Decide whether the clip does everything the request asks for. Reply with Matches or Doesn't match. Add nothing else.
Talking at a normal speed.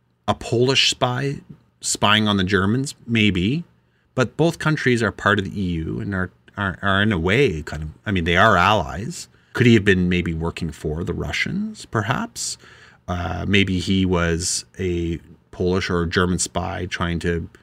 Matches